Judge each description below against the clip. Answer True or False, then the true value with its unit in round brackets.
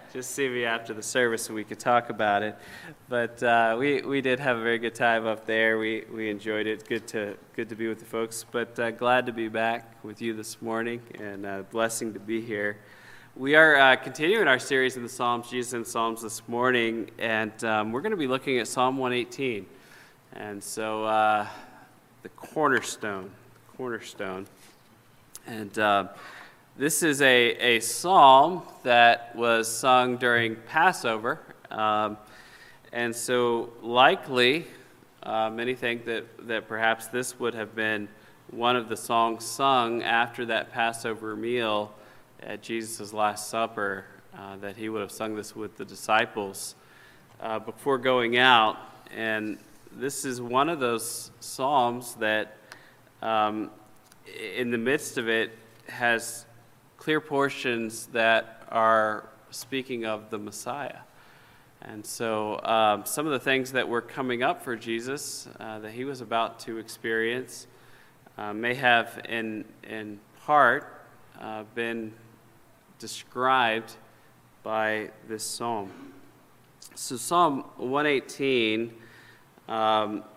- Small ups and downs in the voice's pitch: True (2.1 semitones)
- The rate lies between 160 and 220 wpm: False (145 wpm)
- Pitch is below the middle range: True (115 Hz)